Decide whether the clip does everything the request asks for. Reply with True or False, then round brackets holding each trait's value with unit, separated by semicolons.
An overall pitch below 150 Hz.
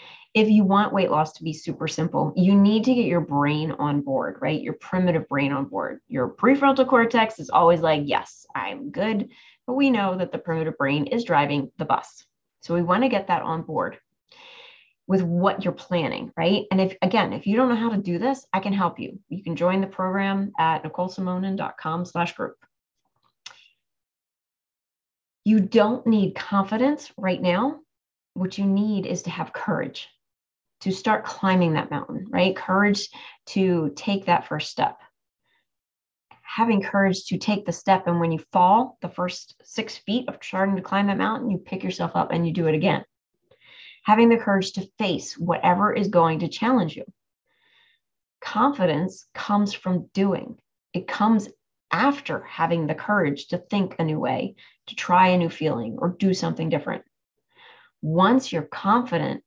False (190 Hz)